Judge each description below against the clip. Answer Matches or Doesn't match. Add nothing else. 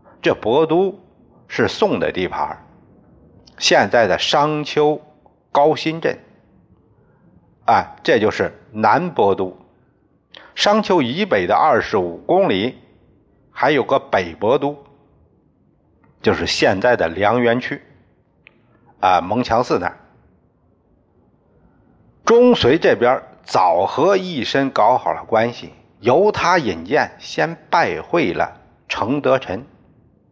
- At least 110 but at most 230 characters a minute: Matches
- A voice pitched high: Doesn't match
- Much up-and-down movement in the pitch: Doesn't match